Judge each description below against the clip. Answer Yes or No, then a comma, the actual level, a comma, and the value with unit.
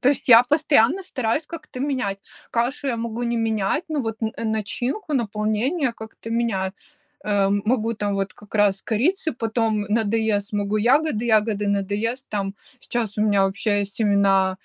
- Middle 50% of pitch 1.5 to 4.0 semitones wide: Yes, average, 3.2 semitones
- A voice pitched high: Yes, high, 220 Hz